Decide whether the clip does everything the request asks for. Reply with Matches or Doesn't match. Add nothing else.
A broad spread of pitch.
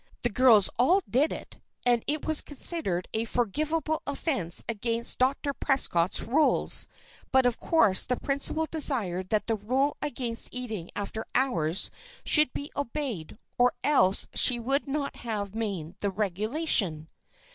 Matches